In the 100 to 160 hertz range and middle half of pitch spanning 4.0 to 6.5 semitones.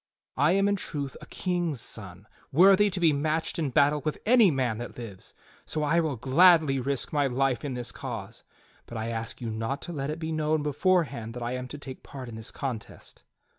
Yes: medium, 140 Hz; average, 4.8 semitones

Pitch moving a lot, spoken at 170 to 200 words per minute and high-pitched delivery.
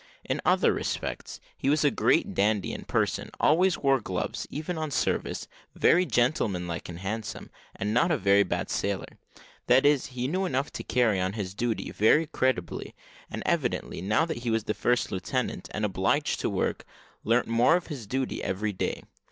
No: wide, 6.1 semitones; average, 185 wpm; low, 120 Hz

